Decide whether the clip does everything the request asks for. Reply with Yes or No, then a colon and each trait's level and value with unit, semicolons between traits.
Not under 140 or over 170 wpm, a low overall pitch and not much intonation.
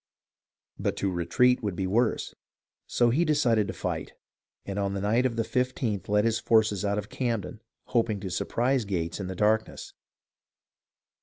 No: average, 165 wpm; low, 110 Hz; average, 3.3 semitones